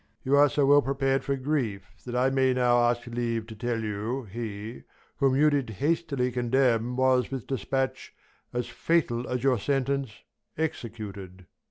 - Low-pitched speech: Yes, low, 125 Hz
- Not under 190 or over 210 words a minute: No, average, 160 wpm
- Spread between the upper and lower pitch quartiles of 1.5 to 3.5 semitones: Yes, average, 2.9 semitones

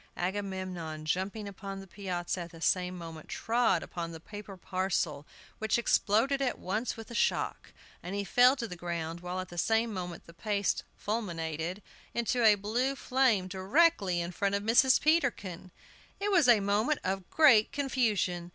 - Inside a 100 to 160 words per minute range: No, average, 170 wpm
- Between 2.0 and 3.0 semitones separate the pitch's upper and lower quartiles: No, average, 4.7 semitones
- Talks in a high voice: Yes, high, 195 Hz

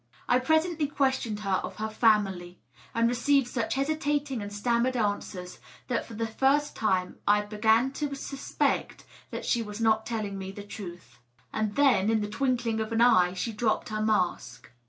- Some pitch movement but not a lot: Yes, average, 3.8 semitones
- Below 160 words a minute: No, average, 175 wpm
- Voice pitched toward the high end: Yes, high, 220 Hz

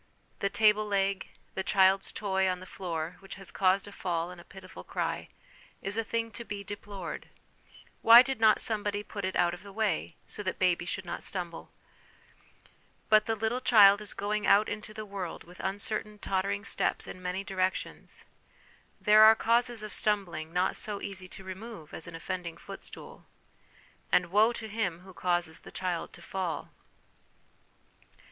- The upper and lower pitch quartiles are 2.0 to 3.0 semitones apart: Yes, narrow, 2.6 semitones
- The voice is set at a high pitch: Yes, high, 195 Hz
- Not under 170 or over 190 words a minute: Yes, average, 175 wpm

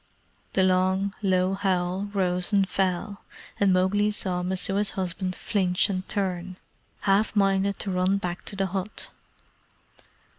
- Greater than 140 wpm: No, slow, 135 wpm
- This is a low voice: No, high, 190 Hz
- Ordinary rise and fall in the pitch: No, narrow, 1.4 semitones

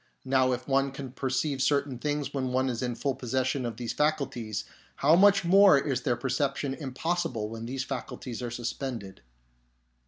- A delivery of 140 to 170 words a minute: Yes, average, 165 wpm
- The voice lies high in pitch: No, low, 130 Hz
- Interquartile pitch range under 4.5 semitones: Yes, narrow, 2.5 semitones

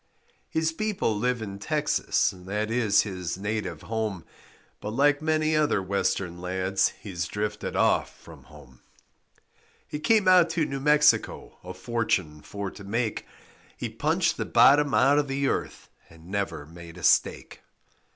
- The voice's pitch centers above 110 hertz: No, low, 105 Hz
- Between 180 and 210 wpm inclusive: No, average, 150 wpm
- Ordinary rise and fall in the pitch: No, wide, 7.7 semitones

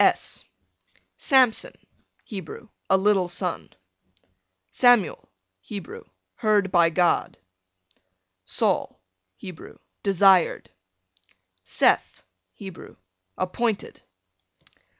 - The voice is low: No, high, 190 Hz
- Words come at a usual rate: No, slow, 70 wpm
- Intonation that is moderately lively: Yes, average, 3.2 semitones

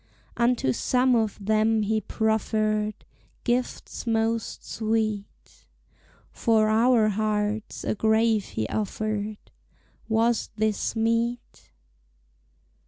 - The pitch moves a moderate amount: No, narrow, 1.1 semitones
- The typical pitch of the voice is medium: No, high, 220 Hz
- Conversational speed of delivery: No, slow, 90 wpm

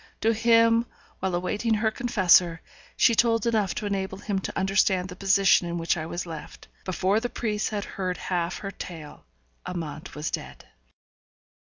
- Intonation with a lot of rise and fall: No, average, 3.7 semitones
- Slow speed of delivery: No, average, 165 wpm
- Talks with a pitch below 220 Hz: Yes, high, 190 Hz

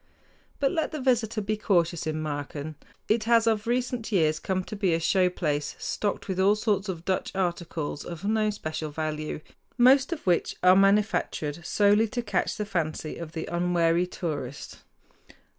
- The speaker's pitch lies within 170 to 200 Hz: Yes, medium, 185 Hz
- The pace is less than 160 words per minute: No, average, 170 wpm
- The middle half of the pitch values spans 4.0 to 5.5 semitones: Yes, average, 4.9 semitones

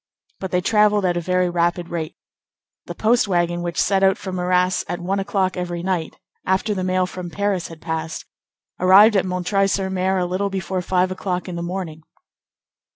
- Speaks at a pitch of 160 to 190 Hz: Yes, medium, 185 Hz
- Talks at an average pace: Yes, average, 190 wpm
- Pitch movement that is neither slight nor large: No, narrow, 1.6 semitones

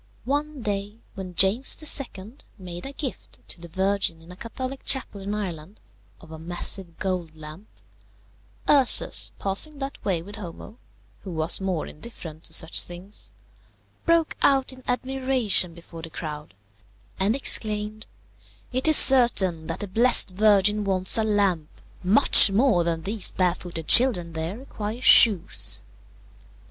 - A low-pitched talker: No, high, 200 Hz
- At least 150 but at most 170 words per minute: No, average, 140 wpm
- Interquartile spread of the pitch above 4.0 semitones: Yes, wide, 5.6 semitones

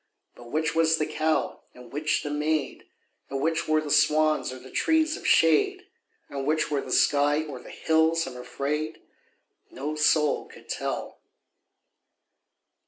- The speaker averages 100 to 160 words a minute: Yes, average, 155 wpm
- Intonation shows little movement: Yes, narrow, 2.1 semitones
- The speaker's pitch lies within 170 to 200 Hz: No, medium, 150 Hz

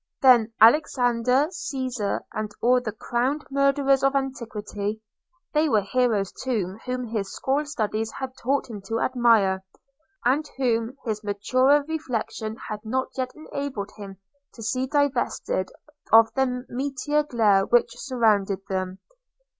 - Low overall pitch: No, high, 245 Hz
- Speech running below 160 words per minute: Yes, average, 140 wpm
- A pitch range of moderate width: Yes, average, 3.8 semitones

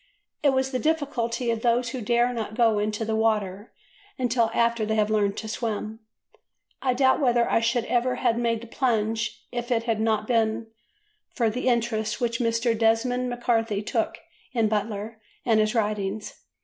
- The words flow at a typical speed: Yes, average, 175 wpm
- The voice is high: Yes, high, 230 Hz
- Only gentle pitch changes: Yes, narrow, 1.8 semitones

